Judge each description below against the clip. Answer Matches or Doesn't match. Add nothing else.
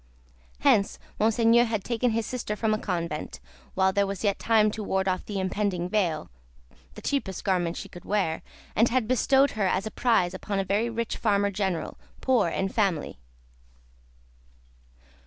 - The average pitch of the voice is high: Matches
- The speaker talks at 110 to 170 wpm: Matches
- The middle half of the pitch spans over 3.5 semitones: Doesn't match